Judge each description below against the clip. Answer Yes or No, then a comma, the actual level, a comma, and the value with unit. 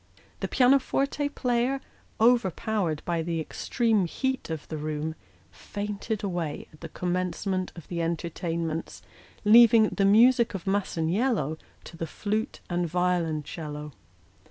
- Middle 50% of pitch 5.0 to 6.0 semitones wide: Yes, average, 5.3 semitones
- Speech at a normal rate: No, slow, 130 wpm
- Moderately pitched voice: Yes, medium, 180 Hz